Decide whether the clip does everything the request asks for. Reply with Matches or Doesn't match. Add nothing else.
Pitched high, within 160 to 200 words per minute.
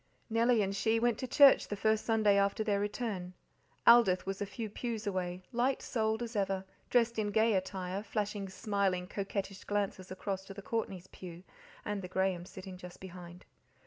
Matches